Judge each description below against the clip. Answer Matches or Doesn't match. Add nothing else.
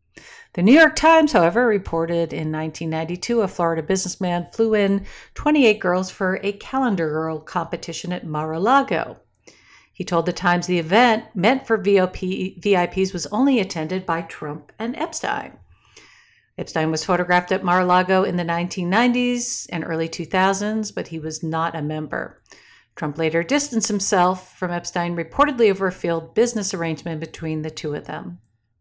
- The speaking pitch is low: Doesn't match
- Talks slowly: Doesn't match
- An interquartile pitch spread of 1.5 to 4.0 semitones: Doesn't match